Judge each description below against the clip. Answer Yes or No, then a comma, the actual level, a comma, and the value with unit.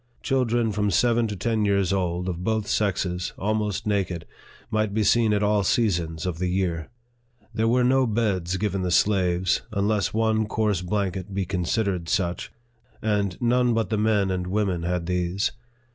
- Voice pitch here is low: Yes, low, 100 Hz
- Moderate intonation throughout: Yes, average, 3.3 semitones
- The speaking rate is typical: Yes, average, 165 wpm